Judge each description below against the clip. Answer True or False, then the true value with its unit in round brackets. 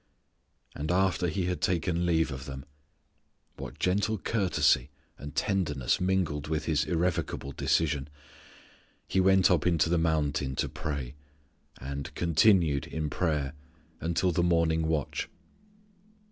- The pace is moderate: False (125 wpm)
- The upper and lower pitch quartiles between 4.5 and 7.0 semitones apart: False (3.6 semitones)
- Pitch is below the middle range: True (80 Hz)